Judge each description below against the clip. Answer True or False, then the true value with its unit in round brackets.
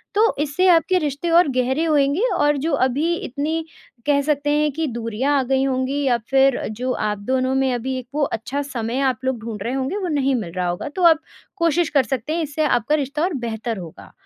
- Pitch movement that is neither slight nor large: True (3.3 semitones)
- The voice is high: True (275 Hz)